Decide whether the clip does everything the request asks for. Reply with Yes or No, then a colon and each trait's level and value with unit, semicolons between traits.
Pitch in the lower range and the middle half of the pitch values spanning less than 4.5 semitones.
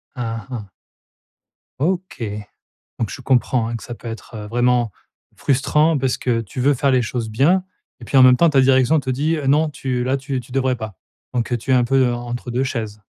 Yes: low, 125 Hz; narrow, 2.4 semitones